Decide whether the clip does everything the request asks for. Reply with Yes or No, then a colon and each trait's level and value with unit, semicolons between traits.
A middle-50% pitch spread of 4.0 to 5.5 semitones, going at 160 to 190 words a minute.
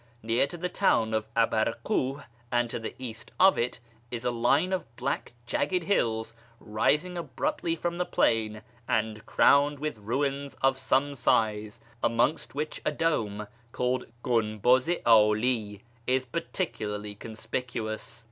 No: average, 4.6 semitones; average, 140 wpm